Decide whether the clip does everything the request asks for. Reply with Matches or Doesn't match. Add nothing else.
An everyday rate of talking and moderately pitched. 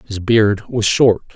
Doesn't match